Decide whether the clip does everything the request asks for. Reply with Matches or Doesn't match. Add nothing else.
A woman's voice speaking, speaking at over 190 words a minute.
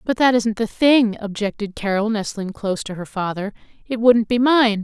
Matches